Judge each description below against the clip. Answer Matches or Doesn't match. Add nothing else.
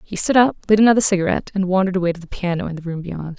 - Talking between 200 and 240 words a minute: Doesn't match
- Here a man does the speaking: Doesn't match